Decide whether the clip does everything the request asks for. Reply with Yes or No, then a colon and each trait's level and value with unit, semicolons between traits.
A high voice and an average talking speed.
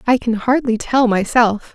Yes: high, 235 Hz; average, 170 wpm